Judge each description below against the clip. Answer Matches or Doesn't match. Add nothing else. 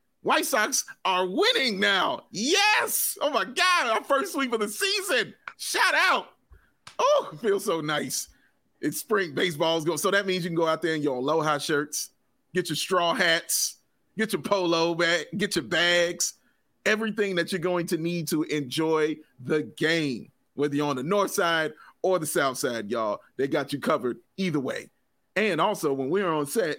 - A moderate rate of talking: Matches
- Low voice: Doesn't match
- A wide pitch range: Doesn't match